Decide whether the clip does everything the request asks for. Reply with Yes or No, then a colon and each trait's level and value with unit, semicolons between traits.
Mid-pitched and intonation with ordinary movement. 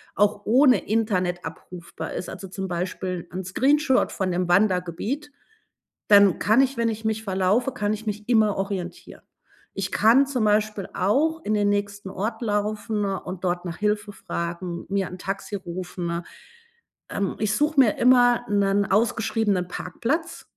No: high, 205 Hz; average, 3.2 semitones